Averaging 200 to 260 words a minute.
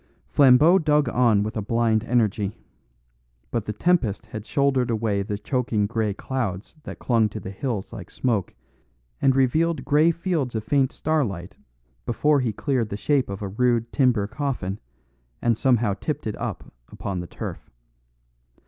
No: average, 155 wpm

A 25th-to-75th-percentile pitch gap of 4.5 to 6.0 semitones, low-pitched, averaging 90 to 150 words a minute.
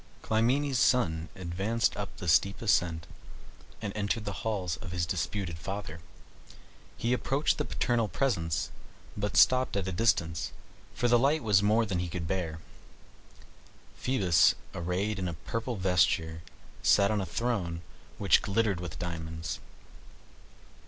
Yes: average, 4.9 semitones; low, 100 Hz; average, 140 wpm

